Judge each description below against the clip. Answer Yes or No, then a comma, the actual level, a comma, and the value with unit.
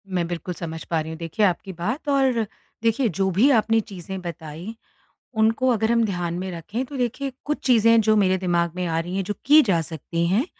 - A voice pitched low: No, high, 195 Hz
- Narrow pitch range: No, average, 5.1 semitones